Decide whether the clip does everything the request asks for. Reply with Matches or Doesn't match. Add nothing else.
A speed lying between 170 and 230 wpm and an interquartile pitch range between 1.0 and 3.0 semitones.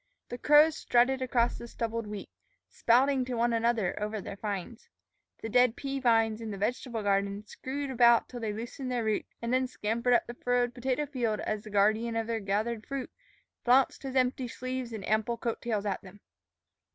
Matches